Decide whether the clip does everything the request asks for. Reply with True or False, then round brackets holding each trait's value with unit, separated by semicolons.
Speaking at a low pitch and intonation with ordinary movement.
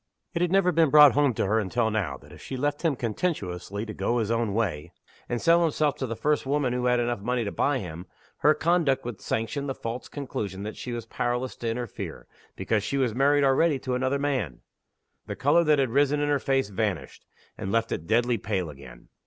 True (125 Hz; 4.9 semitones)